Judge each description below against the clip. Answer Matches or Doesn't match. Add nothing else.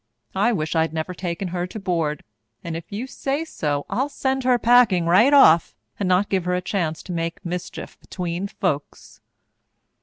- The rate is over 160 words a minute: Matches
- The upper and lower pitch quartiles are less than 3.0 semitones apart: Doesn't match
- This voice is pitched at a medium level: Matches